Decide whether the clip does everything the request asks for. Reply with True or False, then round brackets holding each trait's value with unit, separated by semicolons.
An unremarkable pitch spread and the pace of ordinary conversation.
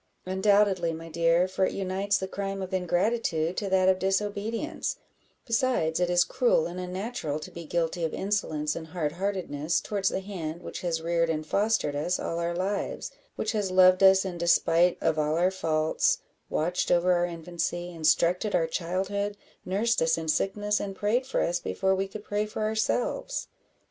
True (3.2 semitones; 175 wpm)